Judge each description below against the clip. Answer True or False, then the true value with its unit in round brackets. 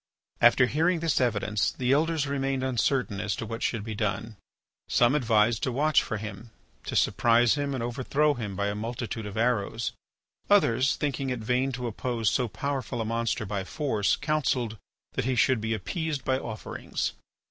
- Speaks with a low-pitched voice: True (120 Hz)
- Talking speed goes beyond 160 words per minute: True (175 wpm)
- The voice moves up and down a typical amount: True (3.6 semitones)